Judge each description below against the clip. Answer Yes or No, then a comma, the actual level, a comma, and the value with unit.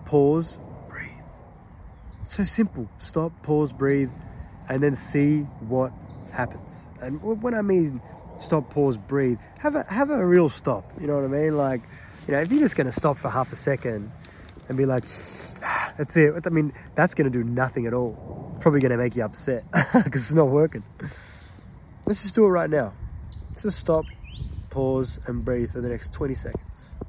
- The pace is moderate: Yes, average, 185 wpm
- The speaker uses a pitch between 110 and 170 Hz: Yes, low, 135 Hz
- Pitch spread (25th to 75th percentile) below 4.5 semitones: No, average, 5.0 semitones